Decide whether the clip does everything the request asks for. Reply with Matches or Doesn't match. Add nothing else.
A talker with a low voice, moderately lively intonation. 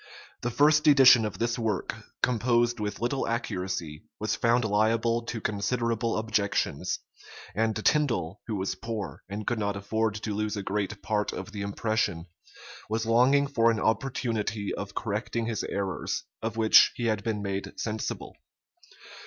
Doesn't match